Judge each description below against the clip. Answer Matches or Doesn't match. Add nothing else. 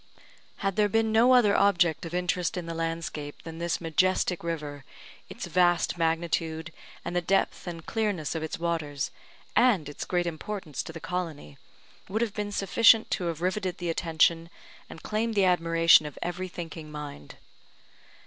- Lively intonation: Doesn't match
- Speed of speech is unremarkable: Matches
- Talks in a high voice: Doesn't match